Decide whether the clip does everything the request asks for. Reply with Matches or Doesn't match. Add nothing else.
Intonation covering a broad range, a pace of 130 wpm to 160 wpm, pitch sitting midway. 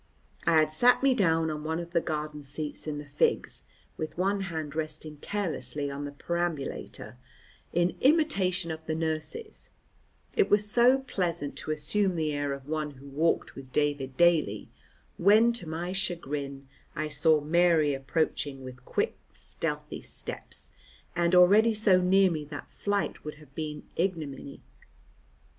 Doesn't match